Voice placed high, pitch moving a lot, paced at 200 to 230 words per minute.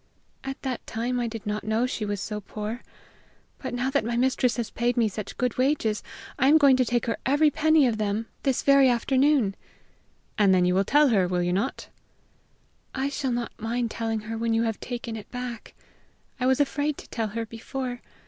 No: high, 240 Hz; average, 3.3 semitones; fast, 205 wpm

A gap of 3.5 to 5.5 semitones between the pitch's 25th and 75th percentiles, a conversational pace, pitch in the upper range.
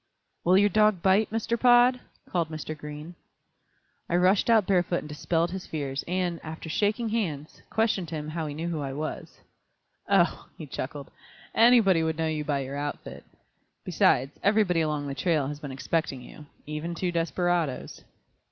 No: average, 4.1 semitones; average, 165 wpm; medium, 165 Hz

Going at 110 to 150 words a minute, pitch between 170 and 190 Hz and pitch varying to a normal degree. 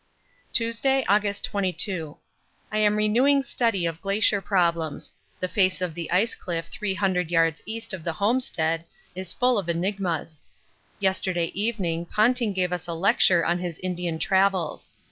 Yes: average, 145 wpm; medium, 185 Hz; average, 3.6 semitones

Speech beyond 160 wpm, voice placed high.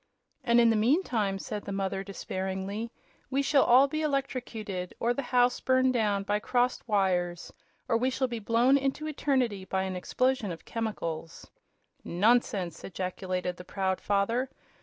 No: average, 155 wpm; high, 220 Hz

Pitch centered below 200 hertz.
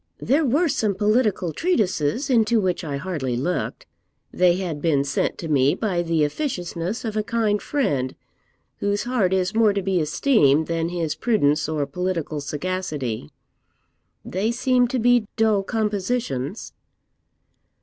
Yes: medium, 185 Hz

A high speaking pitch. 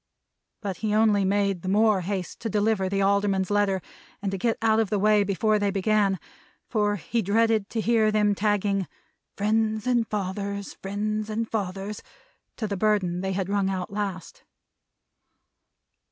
Yes: high, 205 Hz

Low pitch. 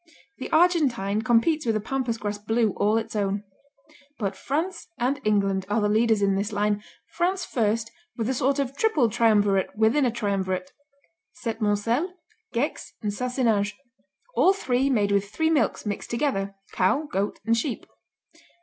No: high, 225 Hz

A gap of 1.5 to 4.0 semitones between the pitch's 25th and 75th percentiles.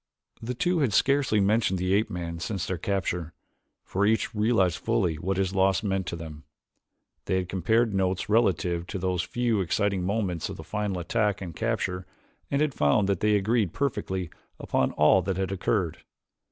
Yes: average, 3.3 semitones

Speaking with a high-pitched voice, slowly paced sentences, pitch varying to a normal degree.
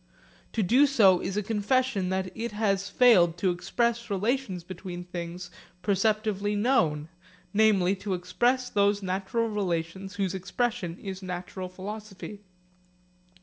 Yes: high, 195 Hz; slow, 125 wpm; average, 3.1 semitones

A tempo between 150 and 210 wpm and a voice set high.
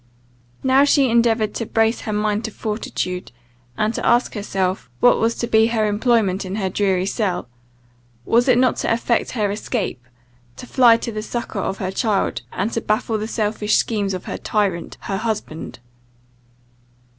Yes: average, 170 wpm; high, 215 Hz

